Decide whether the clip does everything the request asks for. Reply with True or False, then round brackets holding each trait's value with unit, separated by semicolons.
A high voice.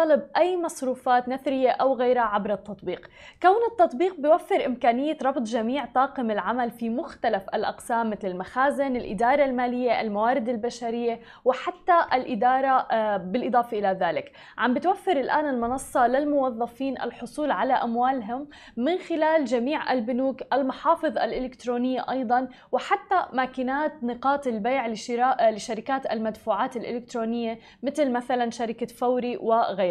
True (255 Hz)